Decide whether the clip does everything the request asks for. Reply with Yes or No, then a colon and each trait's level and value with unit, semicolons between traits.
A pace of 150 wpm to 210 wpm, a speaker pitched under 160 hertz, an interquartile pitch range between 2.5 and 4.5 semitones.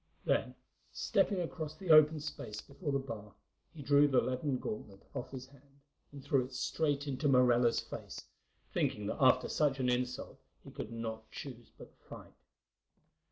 Yes: average, 160 wpm; low, 135 Hz; average, 2.9 semitones